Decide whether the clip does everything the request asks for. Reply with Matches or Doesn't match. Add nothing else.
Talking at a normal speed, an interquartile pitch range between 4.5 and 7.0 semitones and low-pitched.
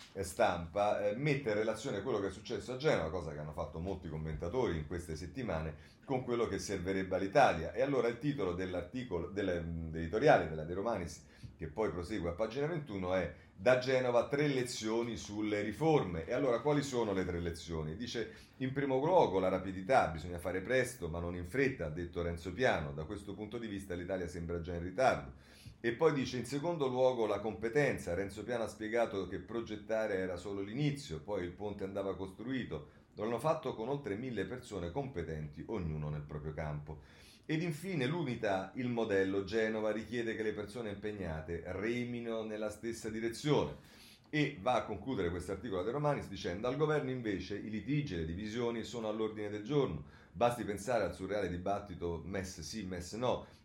Doesn't match